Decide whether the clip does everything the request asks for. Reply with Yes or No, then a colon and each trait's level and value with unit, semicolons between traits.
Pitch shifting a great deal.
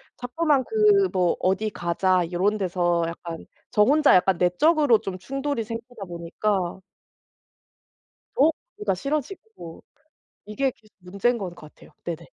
Yes: wide, 7.4 semitones